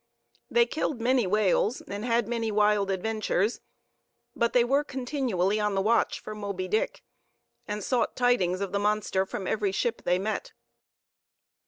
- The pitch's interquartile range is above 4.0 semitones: No, average, 3.3 semitones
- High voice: Yes, high, 215 Hz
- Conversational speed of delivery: Yes, average, 155 wpm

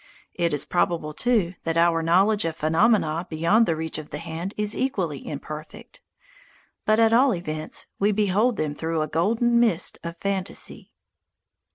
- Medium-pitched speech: Yes, medium, 170 Hz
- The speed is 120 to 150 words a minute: No, average, 160 wpm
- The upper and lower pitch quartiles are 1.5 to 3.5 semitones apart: No, average, 4.8 semitones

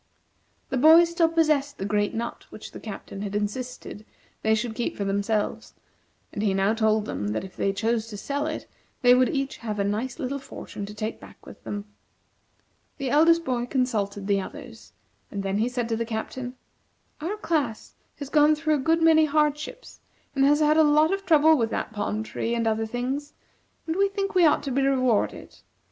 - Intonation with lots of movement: Yes, wide, 6.1 semitones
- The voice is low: No, very high, 250 Hz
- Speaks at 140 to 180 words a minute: No, average, 200 wpm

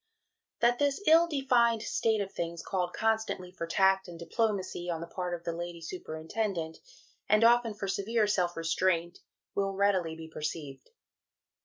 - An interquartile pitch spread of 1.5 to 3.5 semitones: No, average, 4.7 semitones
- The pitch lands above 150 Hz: Yes, high, 190 Hz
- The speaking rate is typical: Yes, average, 160 wpm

